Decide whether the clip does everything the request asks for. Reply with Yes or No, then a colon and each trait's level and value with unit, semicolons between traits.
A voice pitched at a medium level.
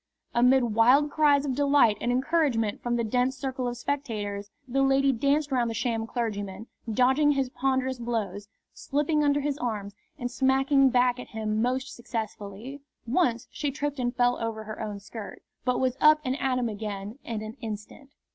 No: very high, 250 Hz